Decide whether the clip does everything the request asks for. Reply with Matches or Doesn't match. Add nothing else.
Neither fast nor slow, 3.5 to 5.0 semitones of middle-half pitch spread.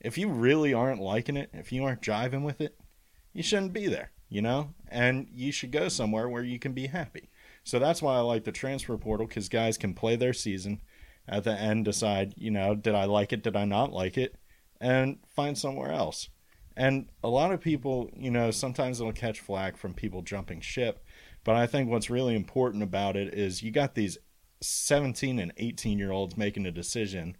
Doesn't match